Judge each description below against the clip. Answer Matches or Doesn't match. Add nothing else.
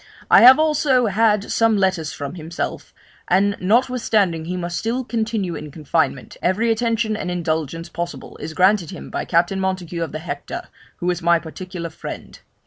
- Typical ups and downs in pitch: Matches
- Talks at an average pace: Matches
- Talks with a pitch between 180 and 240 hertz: Matches